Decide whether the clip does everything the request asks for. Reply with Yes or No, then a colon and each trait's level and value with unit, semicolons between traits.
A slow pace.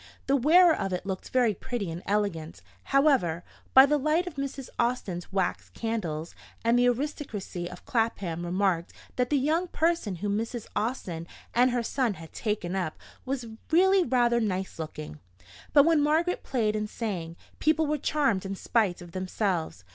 No: average, 165 wpm